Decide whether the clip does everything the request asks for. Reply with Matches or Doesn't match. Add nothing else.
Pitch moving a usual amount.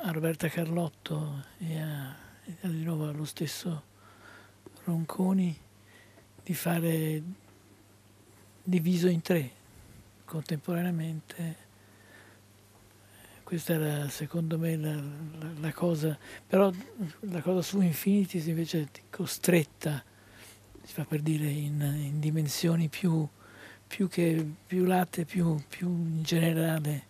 Doesn't match